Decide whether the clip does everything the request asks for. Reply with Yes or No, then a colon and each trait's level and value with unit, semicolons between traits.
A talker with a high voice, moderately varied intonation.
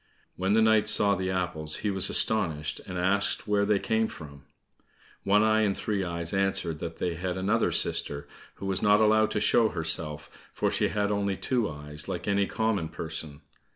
No: very low, 95 Hz; average, 4.0 semitones